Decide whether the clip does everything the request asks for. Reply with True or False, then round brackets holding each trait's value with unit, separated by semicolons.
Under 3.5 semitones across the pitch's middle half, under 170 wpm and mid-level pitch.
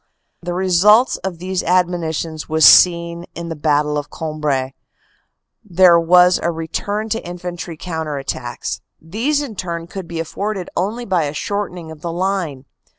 True (2.8 semitones; 150 wpm; 170 Hz)